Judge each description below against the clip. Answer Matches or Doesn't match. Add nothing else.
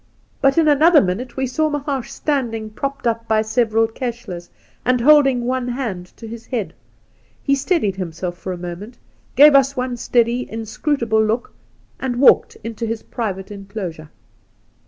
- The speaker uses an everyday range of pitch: Matches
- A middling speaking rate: Matches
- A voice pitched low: Doesn't match